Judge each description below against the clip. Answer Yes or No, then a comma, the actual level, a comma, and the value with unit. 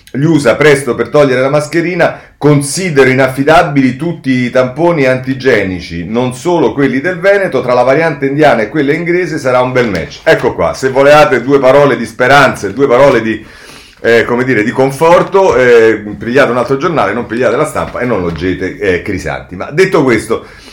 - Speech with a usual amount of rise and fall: Yes, average, 4.5 semitones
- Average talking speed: No, fast, 180 wpm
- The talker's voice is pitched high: No, low, 135 Hz